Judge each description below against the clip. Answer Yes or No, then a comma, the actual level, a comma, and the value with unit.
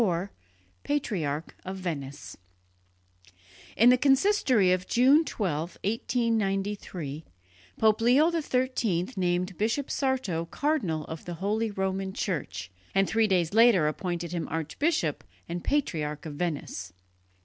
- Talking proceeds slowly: Yes, slow, 115 wpm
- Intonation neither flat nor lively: No, wide, 6.0 semitones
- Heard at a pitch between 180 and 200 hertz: Yes, high, 190 Hz